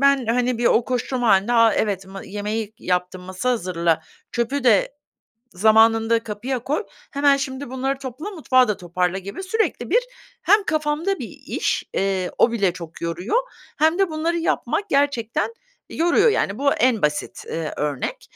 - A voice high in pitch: Yes, high, 235 Hz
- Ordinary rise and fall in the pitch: No, wide, 6.4 semitones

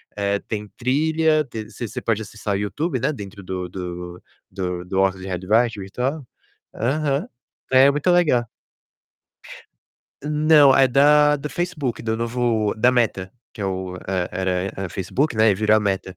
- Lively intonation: Yes, wide, 6.4 semitones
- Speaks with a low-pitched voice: Yes, low, 115 Hz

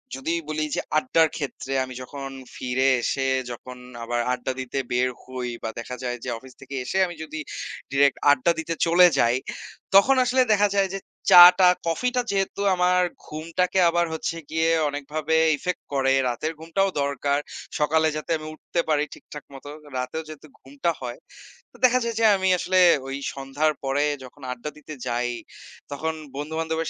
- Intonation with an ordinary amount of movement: Yes, average, 4.2 semitones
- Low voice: No, medium, 155 Hz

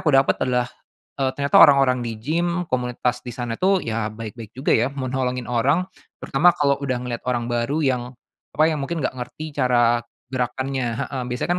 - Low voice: Yes, low, 130 Hz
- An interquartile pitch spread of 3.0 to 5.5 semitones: No, narrow, 2.6 semitones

